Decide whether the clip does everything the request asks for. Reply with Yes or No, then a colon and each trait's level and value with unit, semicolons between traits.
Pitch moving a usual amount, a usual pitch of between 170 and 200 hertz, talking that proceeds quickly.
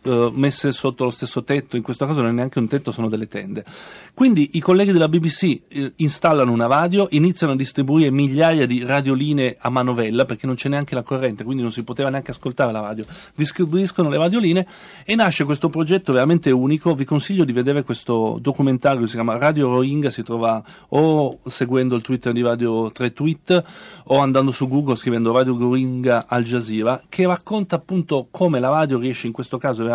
No: average, 4.2 semitones; low, 135 Hz; fast, 190 wpm